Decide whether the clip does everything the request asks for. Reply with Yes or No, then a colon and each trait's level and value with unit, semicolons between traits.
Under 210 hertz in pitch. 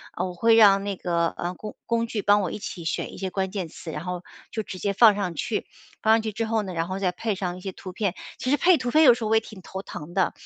Yes: high, 200 Hz